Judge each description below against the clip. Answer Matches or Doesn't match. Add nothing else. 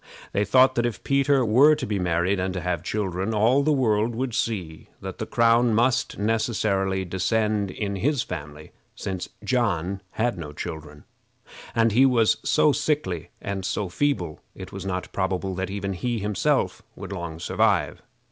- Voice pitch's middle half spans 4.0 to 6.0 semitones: Matches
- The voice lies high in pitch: Doesn't match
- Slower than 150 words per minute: Doesn't match